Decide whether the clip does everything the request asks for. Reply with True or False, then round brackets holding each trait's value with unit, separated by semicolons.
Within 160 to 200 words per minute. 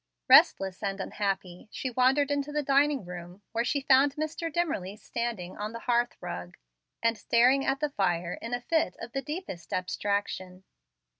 True (165 wpm)